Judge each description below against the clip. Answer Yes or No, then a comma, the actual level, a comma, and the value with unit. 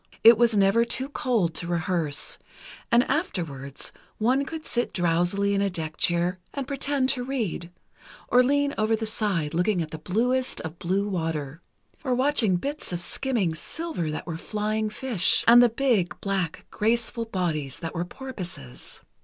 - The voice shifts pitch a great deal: Yes, wide, 6.4 semitones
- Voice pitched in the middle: No, high, 205 Hz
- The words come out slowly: No, average, 160 wpm